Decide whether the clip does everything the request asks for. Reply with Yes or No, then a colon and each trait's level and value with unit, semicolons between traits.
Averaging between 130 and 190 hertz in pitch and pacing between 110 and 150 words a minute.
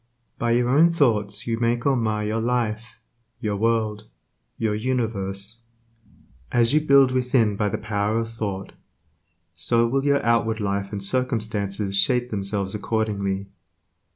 No: low, 110 Hz; average, 140 wpm